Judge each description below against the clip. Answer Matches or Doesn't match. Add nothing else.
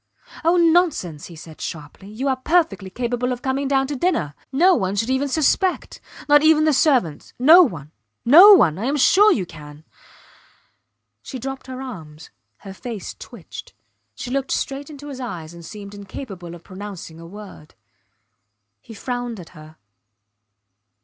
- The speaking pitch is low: Doesn't match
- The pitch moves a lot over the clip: Matches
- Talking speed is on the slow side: Doesn't match